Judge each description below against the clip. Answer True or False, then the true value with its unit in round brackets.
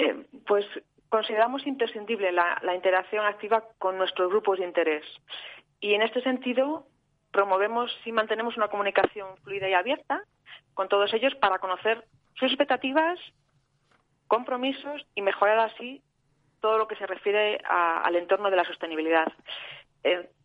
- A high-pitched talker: True (205 Hz)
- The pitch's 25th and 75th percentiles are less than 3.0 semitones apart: False (3.9 semitones)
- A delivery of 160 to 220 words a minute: False (140 wpm)